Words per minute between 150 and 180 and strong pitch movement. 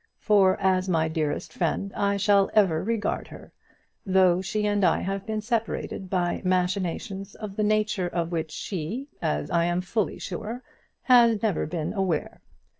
No: average, 160 wpm; average, 3.2 semitones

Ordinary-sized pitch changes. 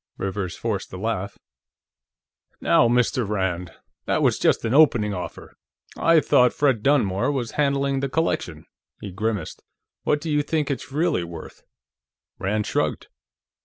No: wide, 6.4 semitones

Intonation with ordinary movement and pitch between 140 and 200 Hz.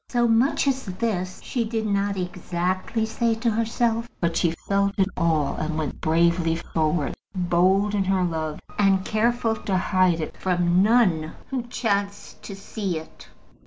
Yes: average, 4.5 semitones; high, 190 Hz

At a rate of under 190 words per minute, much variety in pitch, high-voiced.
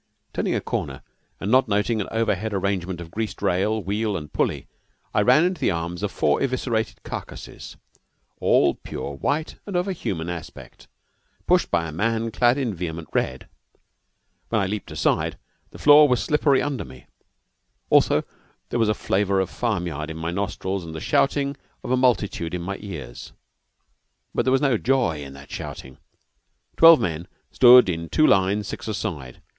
No: average, 175 wpm; wide, 6.4 semitones; low, 100 Hz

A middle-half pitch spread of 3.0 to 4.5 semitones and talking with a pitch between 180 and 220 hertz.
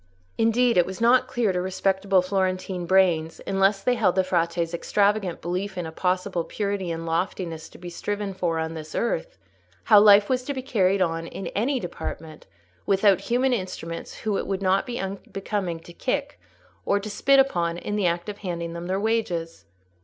Yes: average, 3.3 semitones; high, 190 Hz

